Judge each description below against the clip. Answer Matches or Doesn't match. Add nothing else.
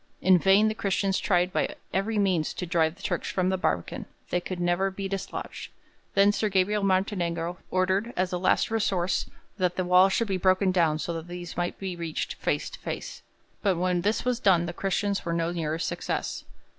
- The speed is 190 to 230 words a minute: Matches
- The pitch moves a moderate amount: Doesn't match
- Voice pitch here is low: Doesn't match